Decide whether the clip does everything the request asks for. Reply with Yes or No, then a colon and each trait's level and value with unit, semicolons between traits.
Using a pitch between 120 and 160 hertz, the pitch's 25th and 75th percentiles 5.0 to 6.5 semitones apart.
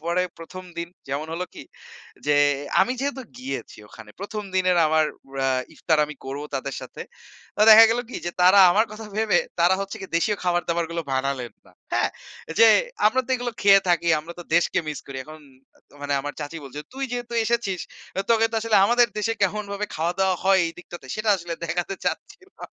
No: medium, 180 Hz; wide, 5.4 semitones